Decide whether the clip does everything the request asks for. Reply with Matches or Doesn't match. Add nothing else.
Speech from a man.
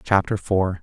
Matches